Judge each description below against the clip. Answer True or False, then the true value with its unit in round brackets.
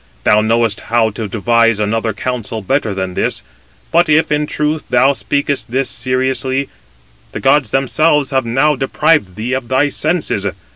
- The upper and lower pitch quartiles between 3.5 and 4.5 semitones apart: True (4.1 semitones)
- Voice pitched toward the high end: False (130 Hz)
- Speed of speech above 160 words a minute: False (155 wpm)